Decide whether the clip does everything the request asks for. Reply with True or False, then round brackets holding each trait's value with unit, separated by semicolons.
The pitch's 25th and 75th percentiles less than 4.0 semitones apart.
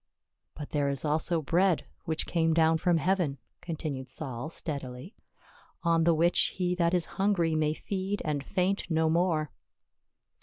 True (2.7 semitones)